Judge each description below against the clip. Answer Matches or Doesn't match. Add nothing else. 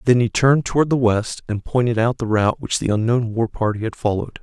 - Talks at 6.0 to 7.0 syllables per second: Matches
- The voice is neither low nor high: Doesn't match